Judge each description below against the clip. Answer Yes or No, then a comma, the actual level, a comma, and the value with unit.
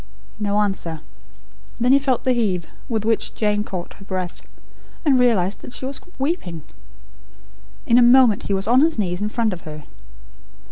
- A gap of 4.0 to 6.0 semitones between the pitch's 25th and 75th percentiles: Yes, average, 4.9 semitones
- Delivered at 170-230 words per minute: Yes, average, 175 wpm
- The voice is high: Yes, high, 210 Hz